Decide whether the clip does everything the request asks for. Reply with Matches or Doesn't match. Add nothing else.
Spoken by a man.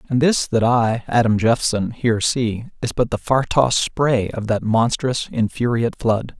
Matches